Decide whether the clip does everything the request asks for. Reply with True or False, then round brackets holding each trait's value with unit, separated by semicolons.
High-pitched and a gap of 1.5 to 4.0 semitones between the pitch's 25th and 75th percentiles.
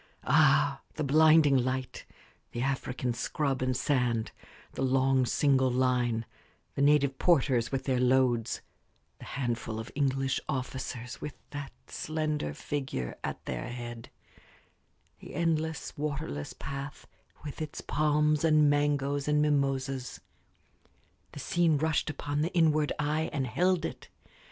False (140 Hz; 2.8 semitones)